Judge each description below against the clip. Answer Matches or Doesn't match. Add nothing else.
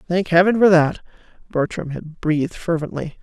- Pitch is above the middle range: Doesn't match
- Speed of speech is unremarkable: Matches